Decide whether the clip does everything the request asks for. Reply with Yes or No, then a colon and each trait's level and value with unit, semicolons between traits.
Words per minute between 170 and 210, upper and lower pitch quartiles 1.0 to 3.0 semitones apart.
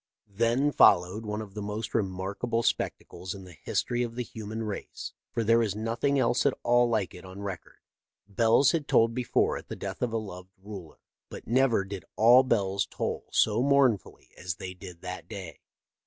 No: average, 185 wpm; average, 3.6 semitones